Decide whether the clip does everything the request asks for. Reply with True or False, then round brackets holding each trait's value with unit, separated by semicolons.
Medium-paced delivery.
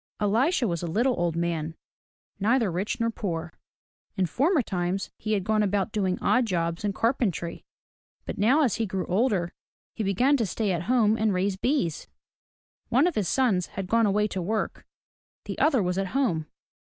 True (180 wpm)